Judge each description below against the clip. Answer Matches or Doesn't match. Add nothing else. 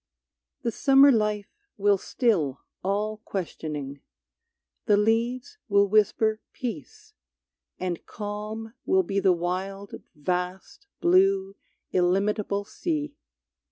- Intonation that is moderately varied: Matches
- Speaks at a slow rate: Matches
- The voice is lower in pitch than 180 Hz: Doesn't match